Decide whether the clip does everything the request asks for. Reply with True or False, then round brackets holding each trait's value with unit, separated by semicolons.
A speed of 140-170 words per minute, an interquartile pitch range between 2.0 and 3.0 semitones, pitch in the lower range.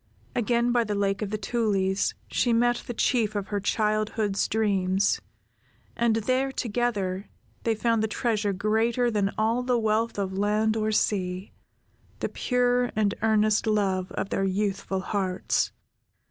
False (145 wpm; 2.7 semitones; 215 Hz)